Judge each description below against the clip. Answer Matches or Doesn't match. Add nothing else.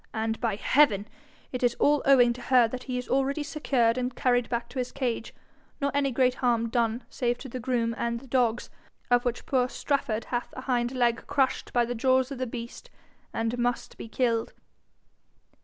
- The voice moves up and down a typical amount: Doesn't match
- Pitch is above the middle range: Matches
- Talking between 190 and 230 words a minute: Matches